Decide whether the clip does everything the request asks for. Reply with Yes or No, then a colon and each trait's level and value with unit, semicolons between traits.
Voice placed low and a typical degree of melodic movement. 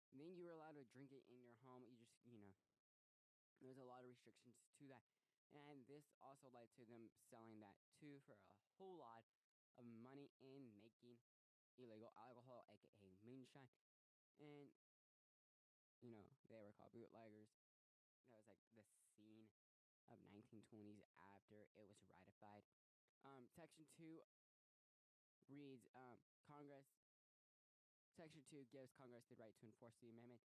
Yes: low, 120 Hz; average, 4.1 semitones